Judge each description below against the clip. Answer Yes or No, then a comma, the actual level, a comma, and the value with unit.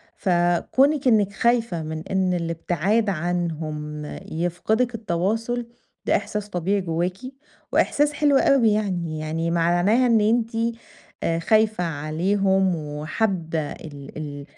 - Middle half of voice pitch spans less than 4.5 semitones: No, average, 5.0 semitones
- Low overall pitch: No, medium, 180 Hz